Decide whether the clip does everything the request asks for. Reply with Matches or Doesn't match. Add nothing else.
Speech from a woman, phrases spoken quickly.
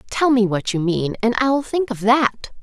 Matches